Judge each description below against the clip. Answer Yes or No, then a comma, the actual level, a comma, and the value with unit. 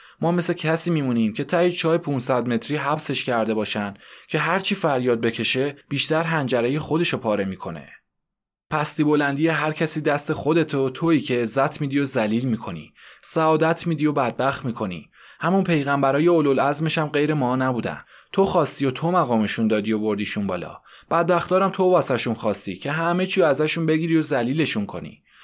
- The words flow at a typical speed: No, fast, 165 wpm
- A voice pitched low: No, medium, 145 Hz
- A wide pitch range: No, average, 4.8 semitones